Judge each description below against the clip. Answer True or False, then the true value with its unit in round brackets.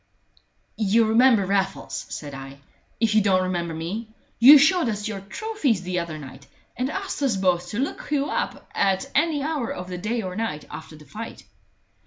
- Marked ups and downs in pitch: True (6.0 semitones)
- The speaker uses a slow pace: False (185 wpm)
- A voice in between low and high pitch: False (205 Hz)